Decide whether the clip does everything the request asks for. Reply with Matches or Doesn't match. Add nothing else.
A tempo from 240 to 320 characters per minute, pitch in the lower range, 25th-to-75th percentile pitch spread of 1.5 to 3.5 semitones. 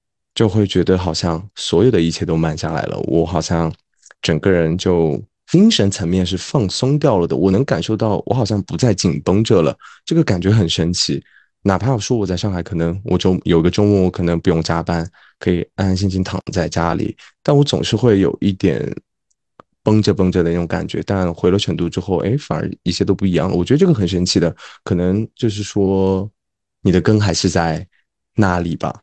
Matches